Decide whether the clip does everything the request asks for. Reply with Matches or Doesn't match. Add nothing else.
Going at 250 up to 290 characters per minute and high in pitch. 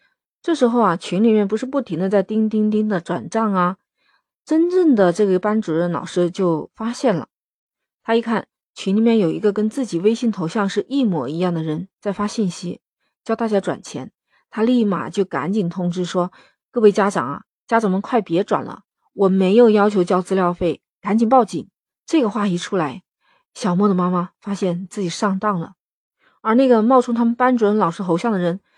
Matches